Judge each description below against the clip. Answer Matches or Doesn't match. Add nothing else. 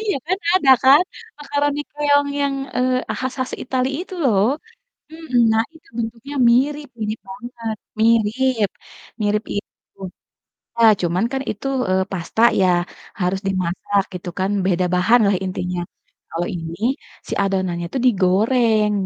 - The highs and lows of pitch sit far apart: Matches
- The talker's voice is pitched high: Matches